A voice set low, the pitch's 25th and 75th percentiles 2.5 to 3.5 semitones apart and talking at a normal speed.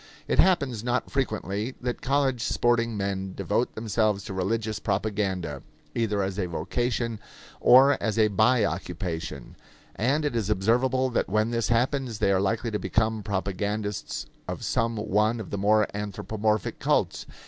Yes: low, 110 Hz; average, 3.1 semitones; average, 150 wpm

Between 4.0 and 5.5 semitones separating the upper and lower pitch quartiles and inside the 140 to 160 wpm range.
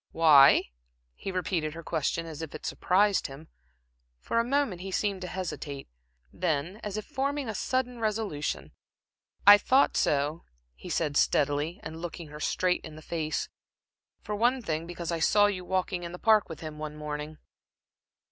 No: average, 5.0 semitones; average, 170 wpm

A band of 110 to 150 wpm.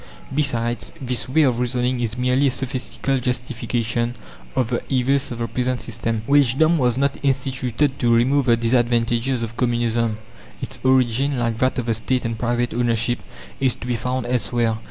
No: average, 170 wpm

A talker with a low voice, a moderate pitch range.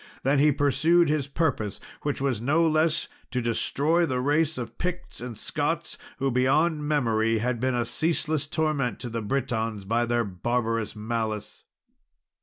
Yes: low, 130 Hz; average, 4.8 semitones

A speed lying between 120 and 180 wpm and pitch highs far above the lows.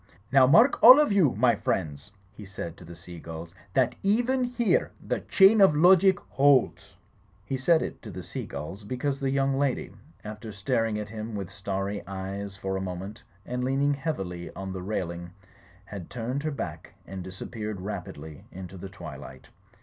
Yes: average, 170 wpm; wide, 6.6 semitones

